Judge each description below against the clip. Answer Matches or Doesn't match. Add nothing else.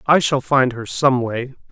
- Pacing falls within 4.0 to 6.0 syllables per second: Matches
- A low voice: Matches